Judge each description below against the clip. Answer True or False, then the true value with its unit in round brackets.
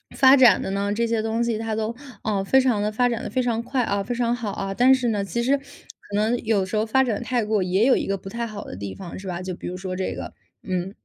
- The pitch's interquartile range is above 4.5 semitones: False (3.6 semitones)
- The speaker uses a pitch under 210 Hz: False (220 Hz)